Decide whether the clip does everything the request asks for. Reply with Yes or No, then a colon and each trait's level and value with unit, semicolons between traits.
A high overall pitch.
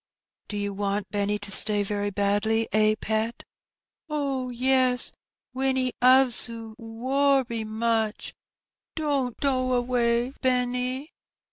Yes: high, 235 Hz